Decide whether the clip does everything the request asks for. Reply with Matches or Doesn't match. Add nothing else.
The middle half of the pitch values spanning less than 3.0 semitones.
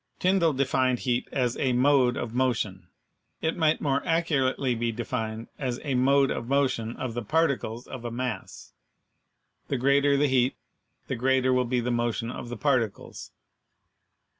Matches